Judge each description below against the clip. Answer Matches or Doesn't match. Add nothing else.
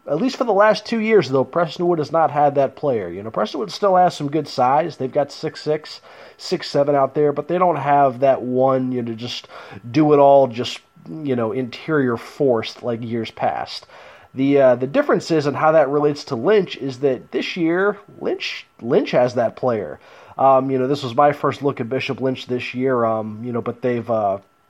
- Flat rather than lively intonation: Doesn't match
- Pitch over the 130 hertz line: Matches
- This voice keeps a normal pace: Doesn't match